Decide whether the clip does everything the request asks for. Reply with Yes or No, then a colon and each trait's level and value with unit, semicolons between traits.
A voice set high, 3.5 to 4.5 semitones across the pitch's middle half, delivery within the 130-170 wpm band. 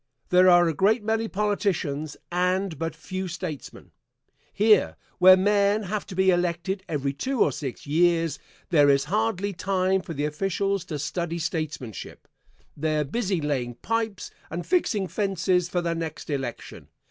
No: medium, 180 Hz; average, 4.0 semitones; average, 155 wpm